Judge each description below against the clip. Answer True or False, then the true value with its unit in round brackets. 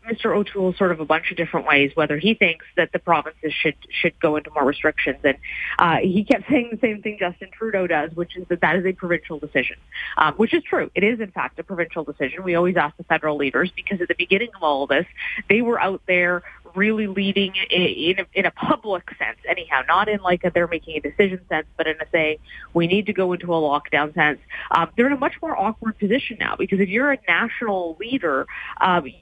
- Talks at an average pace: False (240 wpm)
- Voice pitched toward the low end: False (180 Hz)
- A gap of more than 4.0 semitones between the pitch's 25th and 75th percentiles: True (4.5 semitones)